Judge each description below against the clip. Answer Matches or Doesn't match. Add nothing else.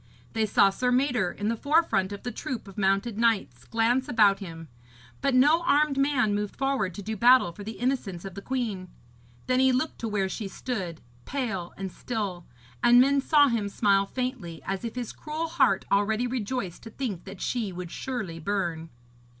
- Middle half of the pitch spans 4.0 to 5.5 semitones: Matches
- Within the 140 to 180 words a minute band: Doesn't match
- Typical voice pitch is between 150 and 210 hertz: Doesn't match